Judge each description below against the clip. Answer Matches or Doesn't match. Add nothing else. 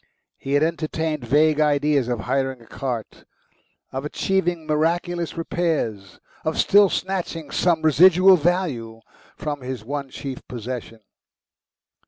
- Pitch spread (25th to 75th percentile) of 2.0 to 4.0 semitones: Doesn't match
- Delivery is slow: Matches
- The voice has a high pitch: Doesn't match